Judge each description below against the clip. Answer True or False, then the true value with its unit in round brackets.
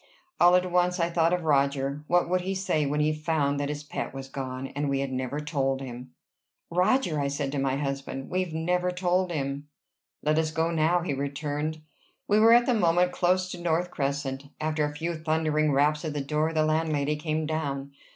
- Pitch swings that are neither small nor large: True (3.6 semitones)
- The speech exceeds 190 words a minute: True (205 wpm)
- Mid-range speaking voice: True (155 Hz)